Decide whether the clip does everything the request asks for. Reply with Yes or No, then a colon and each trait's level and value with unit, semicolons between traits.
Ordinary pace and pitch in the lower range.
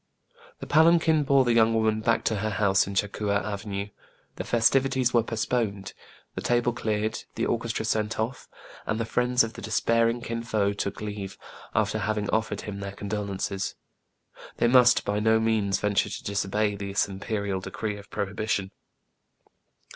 Yes: average, 170 wpm; low, 110 Hz